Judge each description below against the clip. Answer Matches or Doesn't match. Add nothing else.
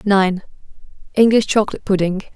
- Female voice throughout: Matches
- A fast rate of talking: Doesn't match